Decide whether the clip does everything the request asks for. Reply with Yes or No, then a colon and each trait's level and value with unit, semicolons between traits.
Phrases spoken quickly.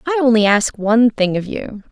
Yes: fast, 220 wpm